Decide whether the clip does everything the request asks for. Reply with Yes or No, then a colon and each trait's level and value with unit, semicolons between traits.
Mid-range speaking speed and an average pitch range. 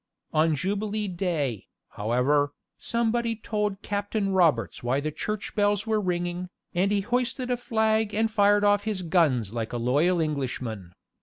No: average, 150 wpm; wide, 6.6 semitones